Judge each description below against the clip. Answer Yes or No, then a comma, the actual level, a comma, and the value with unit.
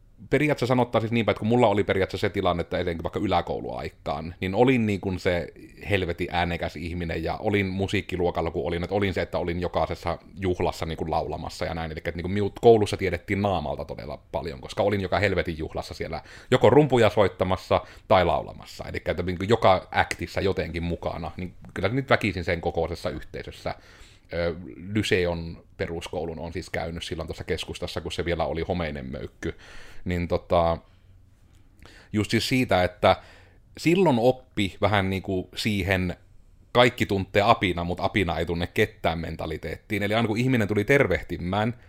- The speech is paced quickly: Yes, fast, 170 wpm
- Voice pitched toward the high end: No, very low, 95 Hz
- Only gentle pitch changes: No, average, 3.2 semitones